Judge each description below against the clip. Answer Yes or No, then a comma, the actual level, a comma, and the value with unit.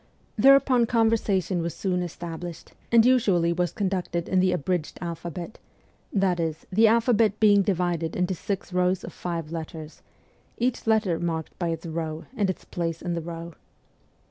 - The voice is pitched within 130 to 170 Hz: No, medium, 180 Hz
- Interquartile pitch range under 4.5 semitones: Yes, average, 3.4 semitones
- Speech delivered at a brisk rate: No, average, 160 wpm